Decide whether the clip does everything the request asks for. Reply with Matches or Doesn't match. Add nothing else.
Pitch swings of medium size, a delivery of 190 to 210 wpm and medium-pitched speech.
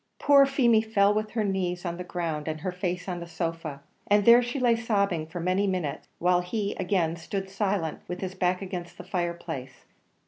Matches